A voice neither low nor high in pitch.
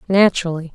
Yes: medium, 180 Hz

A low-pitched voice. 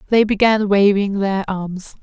No: high, 200 Hz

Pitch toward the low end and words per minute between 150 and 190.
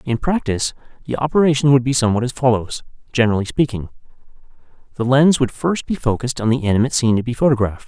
Yes: low, 125 Hz; average, 185 wpm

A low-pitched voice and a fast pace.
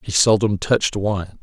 No: low, 100 Hz; average, 170 wpm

